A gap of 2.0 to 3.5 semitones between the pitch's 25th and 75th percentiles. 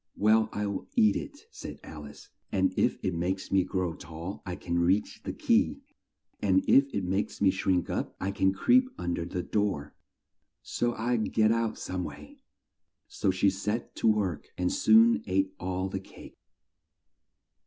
Yes: average, 2.9 semitones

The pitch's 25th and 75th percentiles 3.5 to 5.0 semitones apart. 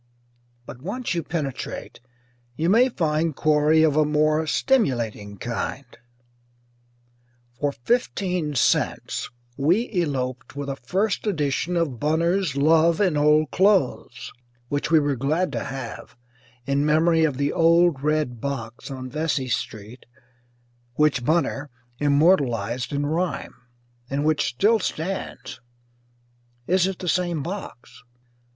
Yes: average, 4.0 semitones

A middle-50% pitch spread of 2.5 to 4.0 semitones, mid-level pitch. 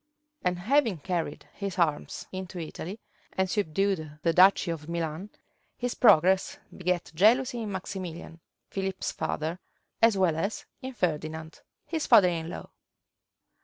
Yes: average, 3.4 semitones; medium, 180 Hz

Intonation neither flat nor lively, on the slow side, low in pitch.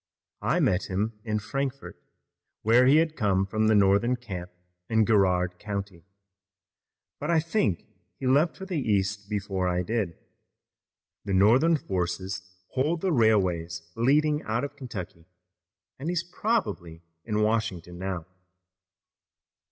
No: wide, 6.2 semitones; slow, 130 wpm; low, 105 Hz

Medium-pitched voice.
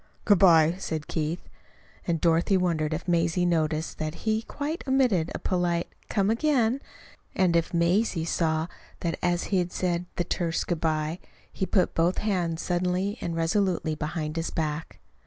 Yes: medium, 170 Hz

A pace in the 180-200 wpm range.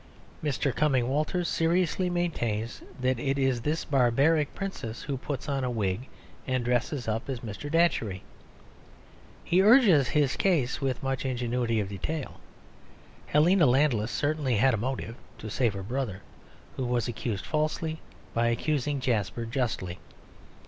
No: average, 140 wpm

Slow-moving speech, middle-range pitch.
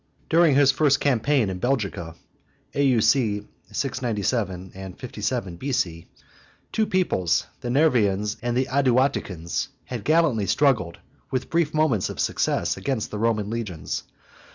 No: slow, 130 wpm; low, 120 Hz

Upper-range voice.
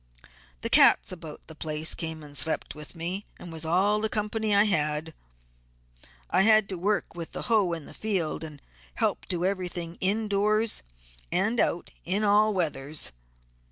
No: medium, 180 Hz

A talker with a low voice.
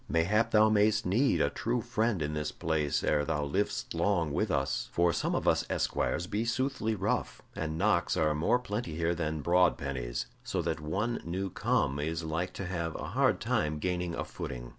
Yes: very low, 85 Hz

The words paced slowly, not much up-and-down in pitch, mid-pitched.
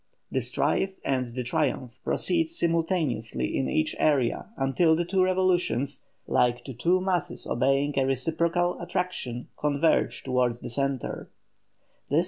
No: slow, 125 wpm; wide, 5.6 semitones; medium, 145 Hz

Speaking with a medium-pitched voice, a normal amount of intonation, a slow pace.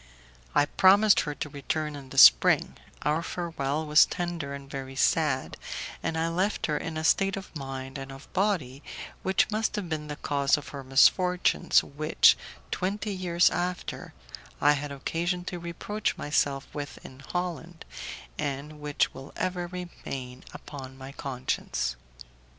No: medium, 150 Hz; average, 4.3 semitones; average, 150 wpm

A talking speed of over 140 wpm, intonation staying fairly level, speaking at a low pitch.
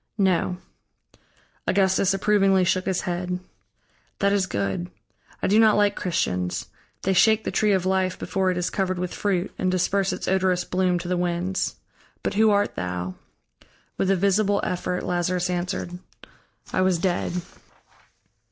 No: average, 150 wpm; narrow, 1.6 semitones; medium, 185 Hz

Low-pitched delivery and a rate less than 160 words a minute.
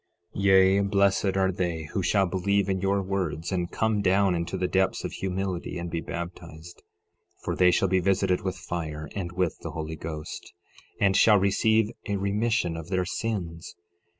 No: very low, 95 Hz; average, 175 wpm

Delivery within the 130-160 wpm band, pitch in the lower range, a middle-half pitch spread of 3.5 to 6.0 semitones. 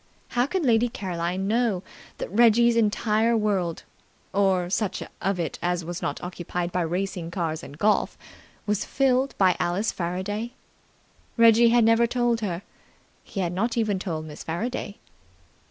No: average, 150 wpm; high, 200 Hz; average, 4.6 semitones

